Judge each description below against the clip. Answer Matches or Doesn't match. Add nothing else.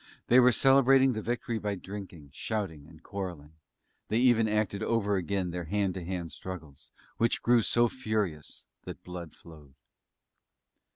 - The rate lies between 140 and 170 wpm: Matches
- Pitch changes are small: Doesn't match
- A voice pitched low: Matches